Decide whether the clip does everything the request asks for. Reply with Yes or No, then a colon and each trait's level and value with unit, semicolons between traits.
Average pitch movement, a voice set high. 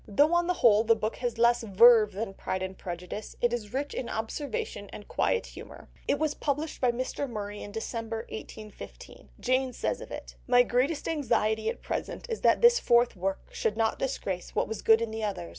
Yes: average, 3.5 semitones; high, 230 Hz